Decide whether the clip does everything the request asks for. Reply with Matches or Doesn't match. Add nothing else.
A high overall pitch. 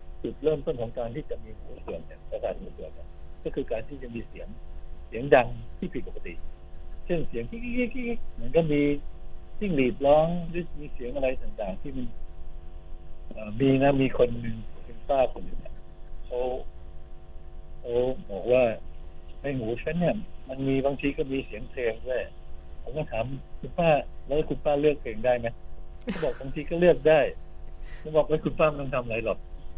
Doesn't match